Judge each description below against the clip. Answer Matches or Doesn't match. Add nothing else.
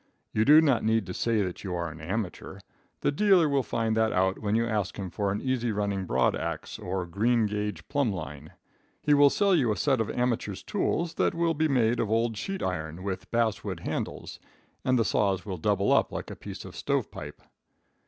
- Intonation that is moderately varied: Matches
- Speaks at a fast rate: Matches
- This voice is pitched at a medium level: Doesn't match